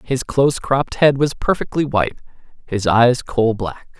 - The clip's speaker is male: Yes, male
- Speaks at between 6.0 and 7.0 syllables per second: No, 5.4 syllables/s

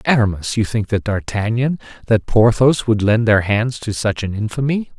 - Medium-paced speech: Yes, average, 180 wpm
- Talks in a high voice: No, low, 115 Hz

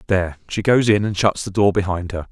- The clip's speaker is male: Yes, male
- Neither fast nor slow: No, fast, 260 wpm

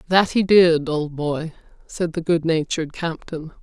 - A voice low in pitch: No, medium, 165 Hz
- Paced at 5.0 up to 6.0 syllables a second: No, 4.4 syllables/s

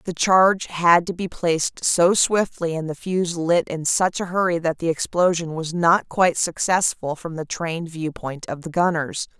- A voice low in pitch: No, medium, 170 Hz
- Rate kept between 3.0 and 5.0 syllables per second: Yes, 4.6 syllables/s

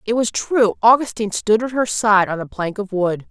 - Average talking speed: No, fast, 235 wpm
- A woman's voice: Yes, female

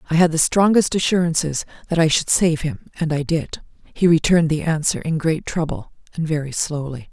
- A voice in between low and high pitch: Yes, medium, 160 Hz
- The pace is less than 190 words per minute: No, average, 195 wpm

